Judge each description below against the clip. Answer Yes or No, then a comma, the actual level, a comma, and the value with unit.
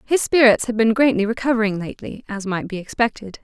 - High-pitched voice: Yes, high, 220 Hz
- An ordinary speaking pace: Yes, average, 190 wpm